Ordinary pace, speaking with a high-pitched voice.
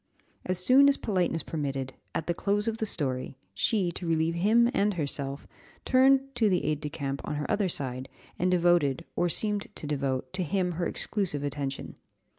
No: average, 185 wpm; medium, 175 Hz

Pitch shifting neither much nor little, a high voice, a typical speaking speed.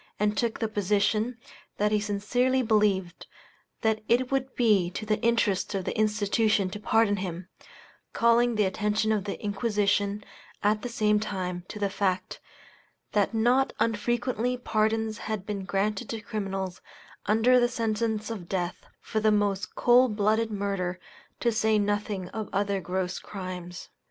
No: narrow, 2.1 semitones; high, 210 Hz; average, 150 wpm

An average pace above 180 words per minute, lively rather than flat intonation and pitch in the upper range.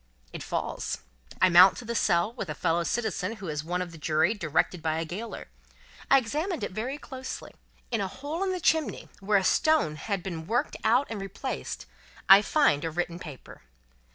Yes: average, 195 wpm; wide, 6.4 semitones; high, 195 Hz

